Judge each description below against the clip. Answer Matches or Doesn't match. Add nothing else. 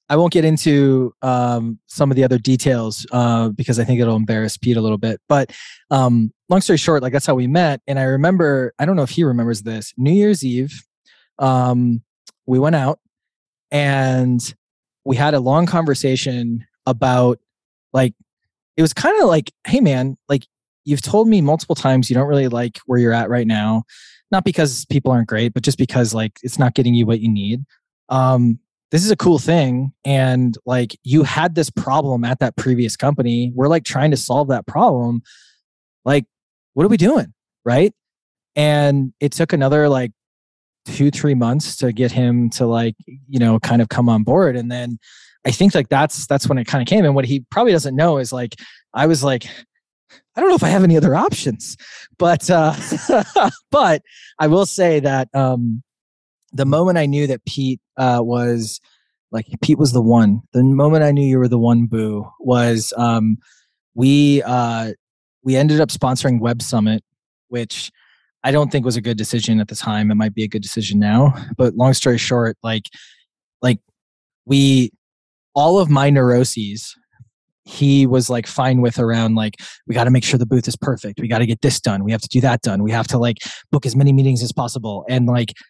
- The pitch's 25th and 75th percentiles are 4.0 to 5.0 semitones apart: Doesn't match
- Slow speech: Doesn't match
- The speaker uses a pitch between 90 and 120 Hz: Doesn't match